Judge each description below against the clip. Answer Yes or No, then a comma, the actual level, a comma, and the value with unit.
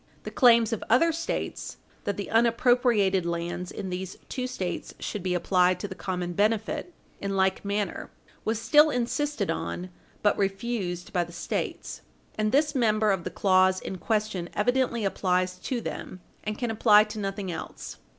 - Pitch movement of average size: Yes, average, 3.9 semitones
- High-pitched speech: Yes, high, 205 Hz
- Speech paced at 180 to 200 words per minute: No, average, 165 wpm